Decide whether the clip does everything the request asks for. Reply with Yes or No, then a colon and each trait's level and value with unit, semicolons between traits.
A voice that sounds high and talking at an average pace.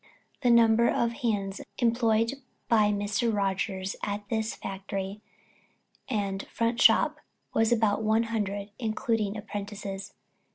No: high, 215 Hz; slow, 115 wpm